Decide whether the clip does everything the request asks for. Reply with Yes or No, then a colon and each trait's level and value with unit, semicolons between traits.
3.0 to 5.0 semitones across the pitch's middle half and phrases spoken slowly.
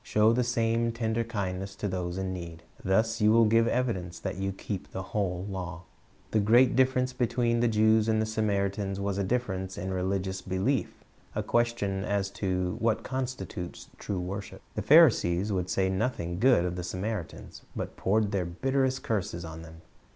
No: average, 3.7 semitones; average, 175 wpm